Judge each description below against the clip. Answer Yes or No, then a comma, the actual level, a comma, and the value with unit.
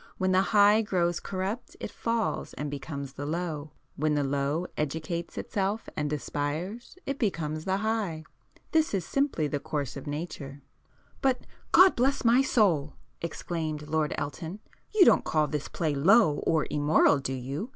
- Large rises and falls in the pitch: Yes, wide, 5.8 semitones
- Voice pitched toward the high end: No, medium, 160 Hz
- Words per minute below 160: Yes, average, 150 wpm